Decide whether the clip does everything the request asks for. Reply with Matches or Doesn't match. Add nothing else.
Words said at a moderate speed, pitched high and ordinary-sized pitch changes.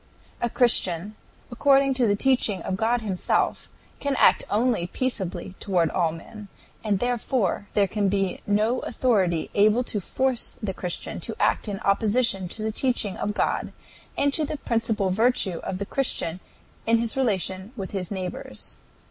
Matches